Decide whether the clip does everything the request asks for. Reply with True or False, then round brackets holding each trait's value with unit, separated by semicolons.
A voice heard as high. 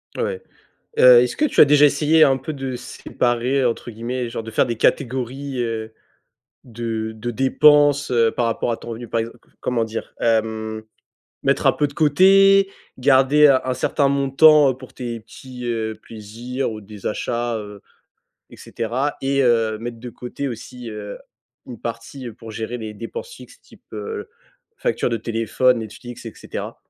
False (120 Hz)